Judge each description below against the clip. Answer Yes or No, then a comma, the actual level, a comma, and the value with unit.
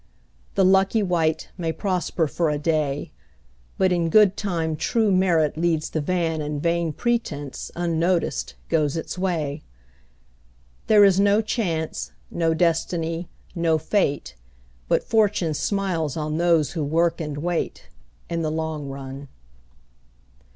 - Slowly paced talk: Yes, slow, 130 wpm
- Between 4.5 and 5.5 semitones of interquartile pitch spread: No, average, 2.9 semitones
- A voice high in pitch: No, medium, 165 Hz